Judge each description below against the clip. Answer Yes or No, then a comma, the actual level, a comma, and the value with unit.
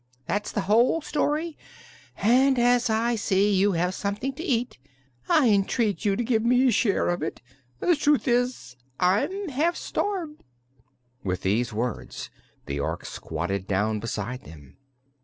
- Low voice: No, high, 215 Hz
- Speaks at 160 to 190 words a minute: No, average, 150 wpm